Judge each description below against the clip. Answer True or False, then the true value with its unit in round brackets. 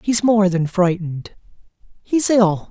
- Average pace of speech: False (110 wpm)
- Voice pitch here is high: True (195 Hz)